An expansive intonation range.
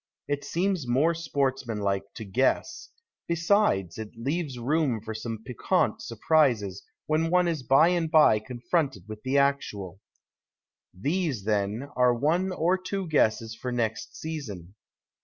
Yes: wide, 6.6 semitones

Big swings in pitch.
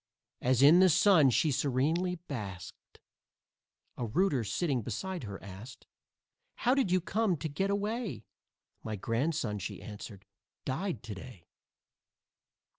Yes: wide, 8.5 semitones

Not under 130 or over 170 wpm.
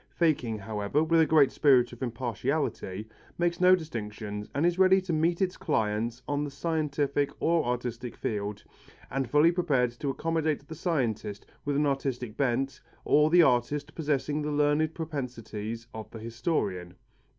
Yes: average, 155 wpm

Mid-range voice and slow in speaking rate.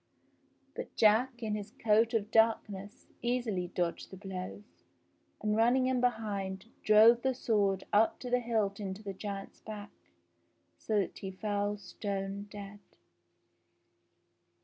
No: high, 210 Hz; slow, 130 wpm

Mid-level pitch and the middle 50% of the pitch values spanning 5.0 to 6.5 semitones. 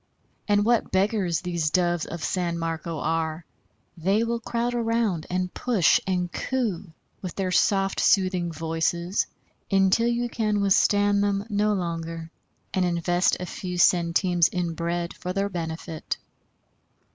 No: medium, 180 Hz; average, 3.2 semitones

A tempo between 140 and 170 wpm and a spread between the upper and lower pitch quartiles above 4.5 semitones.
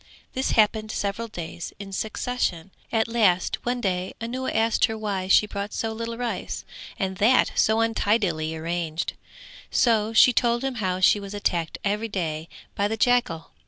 No: average, 160 wpm; average, 3.6 semitones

